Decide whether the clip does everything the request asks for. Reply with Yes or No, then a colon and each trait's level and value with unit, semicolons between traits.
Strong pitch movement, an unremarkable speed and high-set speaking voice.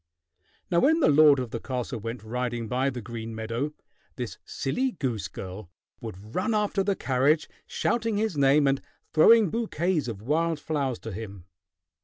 No: wide, 6.6 semitones; average, 165 wpm; low, 135 Hz